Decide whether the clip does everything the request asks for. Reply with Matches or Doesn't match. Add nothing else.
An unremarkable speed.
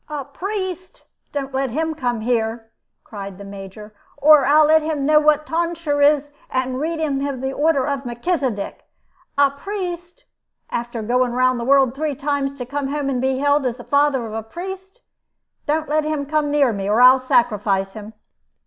Matches